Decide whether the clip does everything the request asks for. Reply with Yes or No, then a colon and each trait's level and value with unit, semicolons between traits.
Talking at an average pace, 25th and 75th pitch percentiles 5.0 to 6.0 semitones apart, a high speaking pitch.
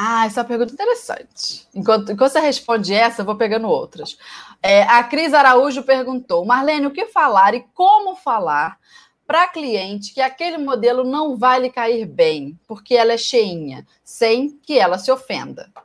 No: average, 175 wpm; average, 4.4 semitones; very high, 250 Hz